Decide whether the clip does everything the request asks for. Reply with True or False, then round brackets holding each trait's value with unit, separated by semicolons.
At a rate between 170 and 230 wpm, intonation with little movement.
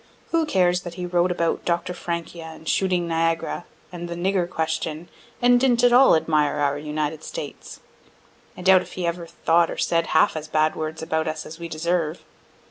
True (190 wpm; 2.0 semitones)